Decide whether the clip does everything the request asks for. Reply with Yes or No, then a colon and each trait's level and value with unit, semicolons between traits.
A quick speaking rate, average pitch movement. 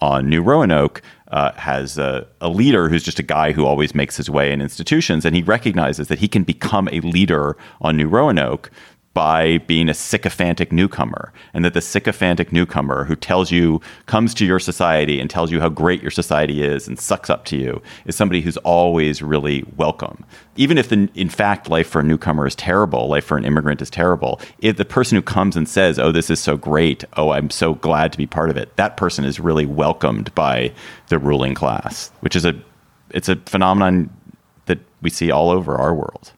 Yes: fast, 210 wpm; average, 3.5 semitones